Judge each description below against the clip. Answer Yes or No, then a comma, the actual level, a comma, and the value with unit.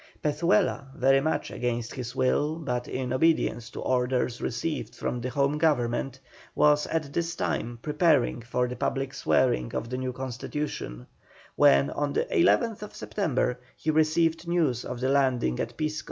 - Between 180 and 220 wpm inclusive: No, average, 155 wpm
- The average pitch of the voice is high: No, low, 135 Hz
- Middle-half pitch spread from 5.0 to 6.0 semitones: No, average, 3.9 semitones